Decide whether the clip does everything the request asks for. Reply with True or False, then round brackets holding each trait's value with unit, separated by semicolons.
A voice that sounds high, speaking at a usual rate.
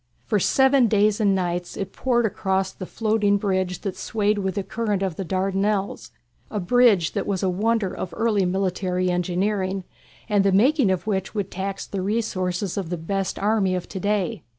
True (195 Hz; 185 wpm)